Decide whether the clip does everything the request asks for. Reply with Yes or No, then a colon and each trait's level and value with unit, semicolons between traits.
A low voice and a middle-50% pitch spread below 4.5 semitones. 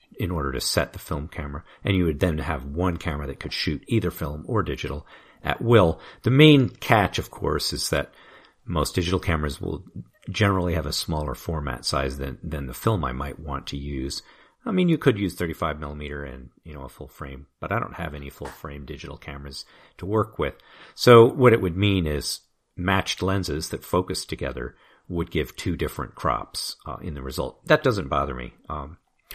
No: very low, 80 Hz; average, 4.8 semitones